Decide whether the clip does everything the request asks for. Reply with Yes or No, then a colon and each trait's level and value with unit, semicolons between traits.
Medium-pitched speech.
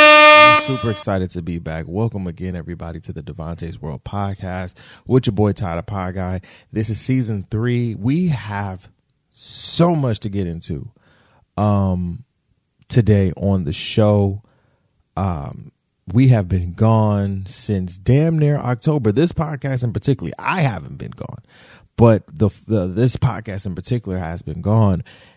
No: low, 105 Hz